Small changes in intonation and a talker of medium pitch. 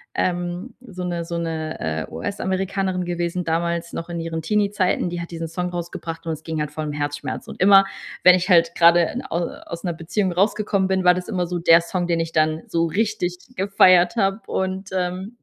Yes: narrow, 2.2 semitones; medium, 175 Hz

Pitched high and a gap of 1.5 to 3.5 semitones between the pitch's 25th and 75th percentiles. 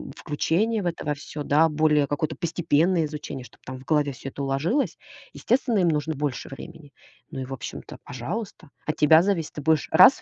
No: medium, 150 Hz; average, 3.0 semitones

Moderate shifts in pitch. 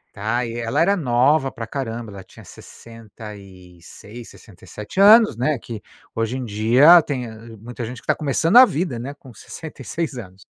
Yes: average, 4.9 semitones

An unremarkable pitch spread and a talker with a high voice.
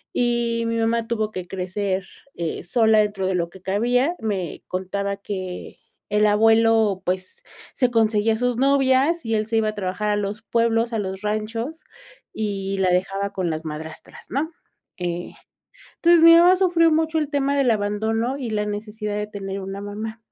Yes: average, 3.3 semitones; high, 215 Hz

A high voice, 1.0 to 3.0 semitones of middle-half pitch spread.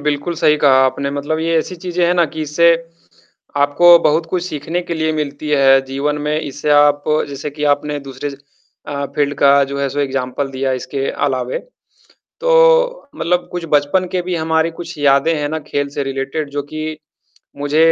No: medium, 150 Hz; average, 2.7 semitones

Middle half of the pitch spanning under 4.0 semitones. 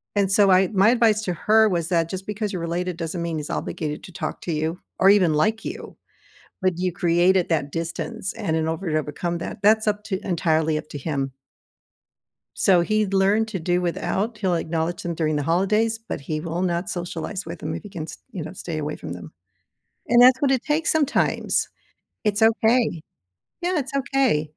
No: average, 4.6 semitones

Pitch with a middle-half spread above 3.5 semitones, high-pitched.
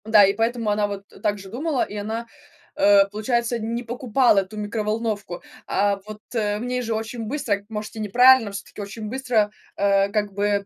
No: narrow, 2.5 semitones; high, 215 Hz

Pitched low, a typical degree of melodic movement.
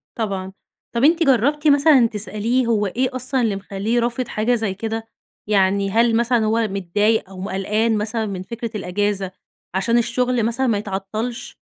No: high, 225 Hz; average, 3.2 semitones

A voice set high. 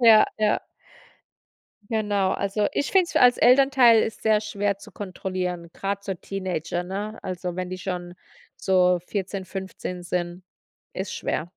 Yes: high, 195 Hz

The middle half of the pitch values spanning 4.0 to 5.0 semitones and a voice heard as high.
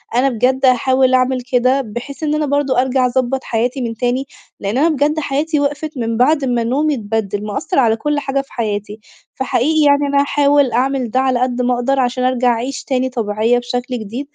No: narrow, 2.4 semitones; very high, 255 Hz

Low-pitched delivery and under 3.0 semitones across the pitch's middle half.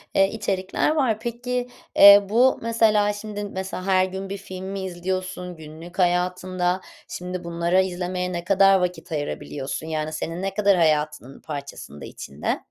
No: medium, 185 Hz; narrow, 2.5 semitones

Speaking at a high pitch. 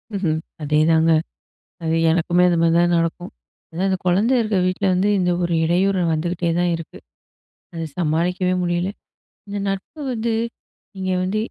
No: medium, 175 Hz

